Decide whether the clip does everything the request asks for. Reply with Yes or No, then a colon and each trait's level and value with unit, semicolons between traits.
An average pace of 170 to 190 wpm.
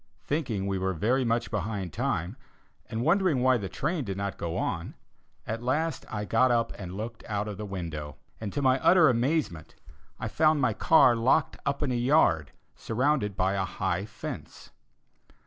Yes: average, 180 wpm